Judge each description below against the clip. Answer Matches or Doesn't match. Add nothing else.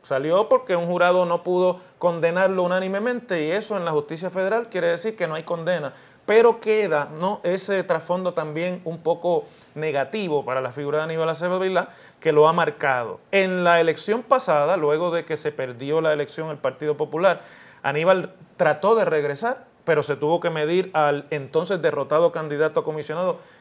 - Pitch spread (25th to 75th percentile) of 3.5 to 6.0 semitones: Doesn't match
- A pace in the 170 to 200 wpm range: Matches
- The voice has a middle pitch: Matches